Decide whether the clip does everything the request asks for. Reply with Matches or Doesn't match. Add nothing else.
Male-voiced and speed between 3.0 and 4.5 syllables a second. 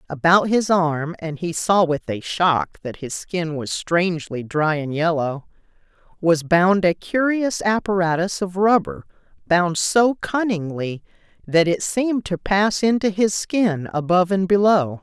Doesn't match